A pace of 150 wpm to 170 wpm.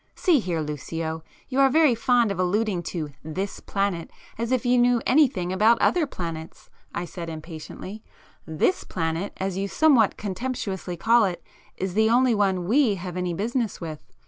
Yes: average, 165 wpm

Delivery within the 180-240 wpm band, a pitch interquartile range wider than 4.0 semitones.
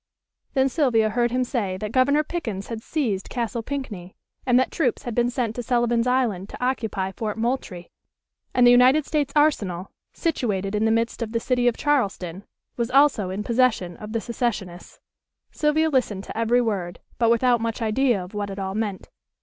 No: average, 185 wpm; average, 3.7 semitones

